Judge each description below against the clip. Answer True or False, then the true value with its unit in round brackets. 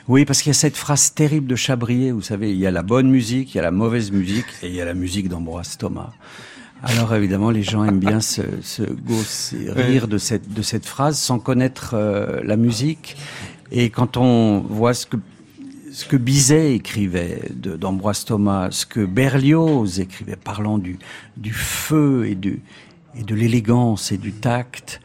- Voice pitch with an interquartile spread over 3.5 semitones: True (4.4 semitones)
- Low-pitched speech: True (115 Hz)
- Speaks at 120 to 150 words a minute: False (195 wpm)